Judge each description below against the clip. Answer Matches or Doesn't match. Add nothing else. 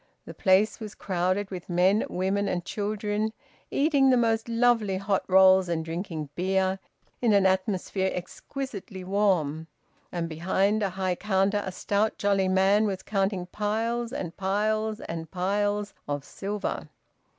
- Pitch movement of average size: Doesn't match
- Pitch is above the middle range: Matches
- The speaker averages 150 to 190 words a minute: Doesn't match